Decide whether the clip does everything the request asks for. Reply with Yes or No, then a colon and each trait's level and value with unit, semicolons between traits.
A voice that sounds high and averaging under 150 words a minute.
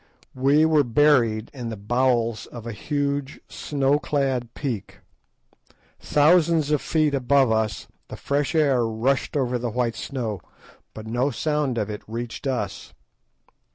No: low, 130 Hz; average, 140 wpm